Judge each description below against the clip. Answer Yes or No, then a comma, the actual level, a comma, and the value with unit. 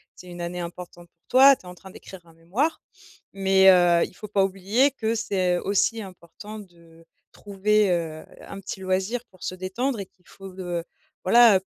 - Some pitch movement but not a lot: Yes, average, 3.1 semitones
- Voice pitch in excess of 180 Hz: Yes, high, 190 Hz